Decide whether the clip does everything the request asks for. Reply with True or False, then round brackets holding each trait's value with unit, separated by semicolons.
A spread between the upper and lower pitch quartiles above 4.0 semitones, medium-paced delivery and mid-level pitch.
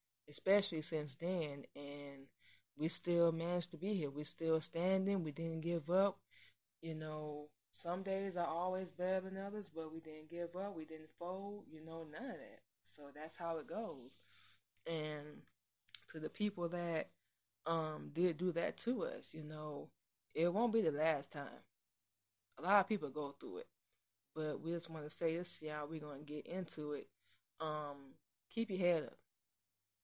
False (3.5 semitones; 180 wpm; 160 Hz)